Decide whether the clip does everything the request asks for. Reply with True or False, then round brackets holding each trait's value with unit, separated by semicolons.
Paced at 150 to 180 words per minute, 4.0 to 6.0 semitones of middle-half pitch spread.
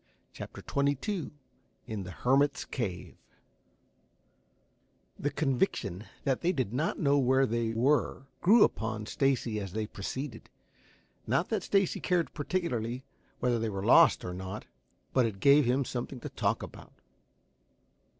False (135 wpm; 4.5 semitones)